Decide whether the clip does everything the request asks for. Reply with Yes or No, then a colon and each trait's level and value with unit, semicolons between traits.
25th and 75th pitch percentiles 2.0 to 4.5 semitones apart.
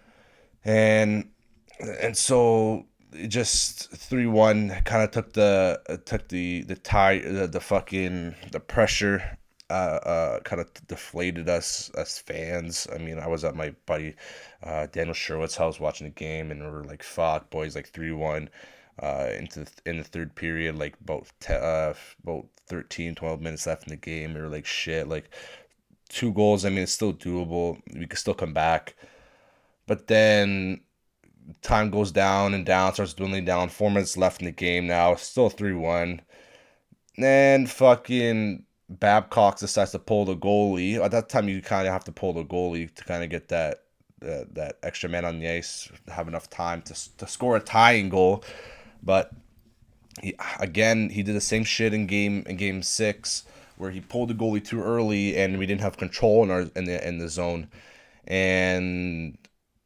Yes: average, 3.8 semitones